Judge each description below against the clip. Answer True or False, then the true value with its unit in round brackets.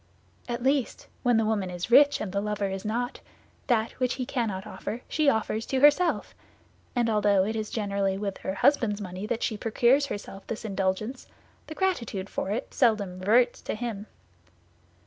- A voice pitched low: False (220 Hz)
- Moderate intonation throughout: True (3.6 semitones)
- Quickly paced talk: False (175 wpm)